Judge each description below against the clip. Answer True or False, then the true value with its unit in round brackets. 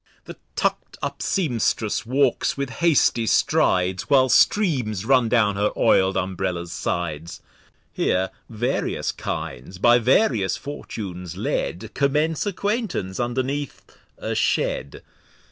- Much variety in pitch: True (6.7 semitones)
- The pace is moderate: False (110 wpm)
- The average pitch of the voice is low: True (115 Hz)